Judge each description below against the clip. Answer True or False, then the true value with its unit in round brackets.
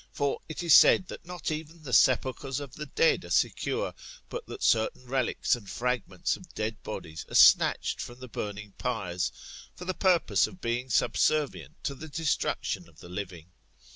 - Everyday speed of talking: True (175 wpm)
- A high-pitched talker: False (130 Hz)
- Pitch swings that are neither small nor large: False (7.0 semitones)